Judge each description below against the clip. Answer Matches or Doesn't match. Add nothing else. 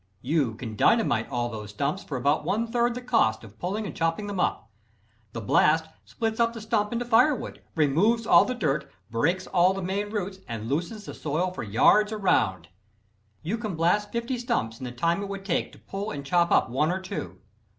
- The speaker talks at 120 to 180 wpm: Doesn't match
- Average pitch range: Doesn't match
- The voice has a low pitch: Doesn't match